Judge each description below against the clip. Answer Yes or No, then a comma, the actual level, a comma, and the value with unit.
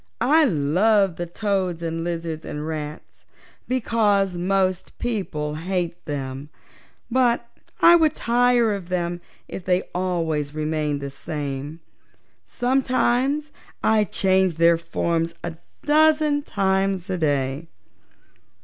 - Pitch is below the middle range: No, medium, 180 Hz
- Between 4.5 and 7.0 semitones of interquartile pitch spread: Yes, wide, 5.6 semitones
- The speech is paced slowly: Yes, slow, 115 wpm